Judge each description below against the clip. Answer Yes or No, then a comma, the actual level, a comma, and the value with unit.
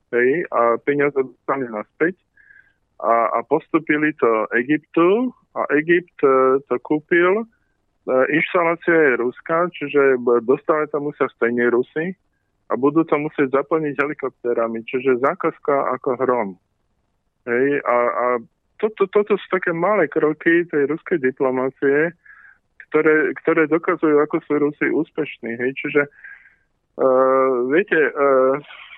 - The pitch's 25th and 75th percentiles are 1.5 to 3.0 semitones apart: No, average, 4.1 semitones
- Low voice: No, medium, 145 Hz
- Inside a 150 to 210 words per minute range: No, average, 125 wpm